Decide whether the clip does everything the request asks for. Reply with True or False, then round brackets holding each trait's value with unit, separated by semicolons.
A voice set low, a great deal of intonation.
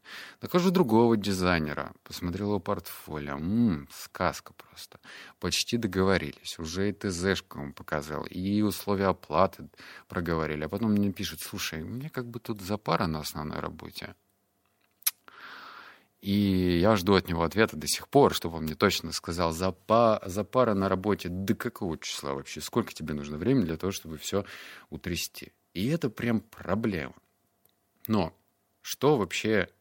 False (95 Hz; 4.5 semitones)